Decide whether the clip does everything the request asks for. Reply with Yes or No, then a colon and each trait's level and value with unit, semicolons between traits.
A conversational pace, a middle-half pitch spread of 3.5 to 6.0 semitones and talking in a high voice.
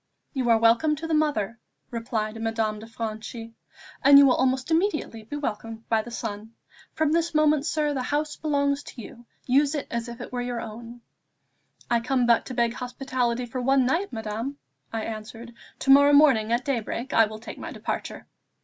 Yes: average, 190 wpm; average, 3.8 semitones; high, 245 Hz